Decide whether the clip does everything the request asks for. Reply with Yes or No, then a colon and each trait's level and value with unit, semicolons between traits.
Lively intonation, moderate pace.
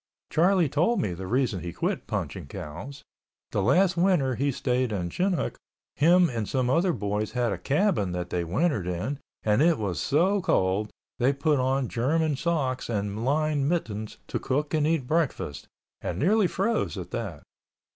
Yes: wide, 7.9 semitones; average, 170 wpm